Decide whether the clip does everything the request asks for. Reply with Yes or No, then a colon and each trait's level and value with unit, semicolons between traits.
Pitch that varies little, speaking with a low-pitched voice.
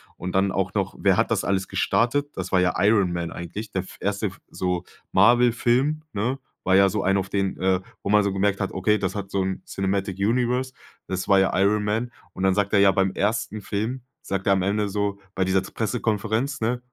Yes: narrow, 2.3 semitones; low, 100 Hz